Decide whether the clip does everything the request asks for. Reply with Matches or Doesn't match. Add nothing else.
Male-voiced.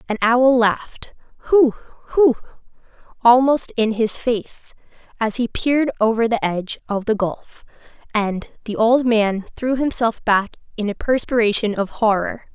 Doesn't match